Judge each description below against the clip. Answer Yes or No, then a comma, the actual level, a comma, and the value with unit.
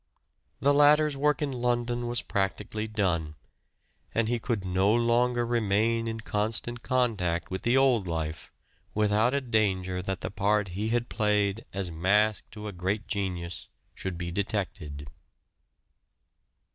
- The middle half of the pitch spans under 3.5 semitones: No, average, 4.0 semitones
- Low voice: Yes, low, 105 Hz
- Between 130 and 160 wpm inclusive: Yes, average, 140 wpm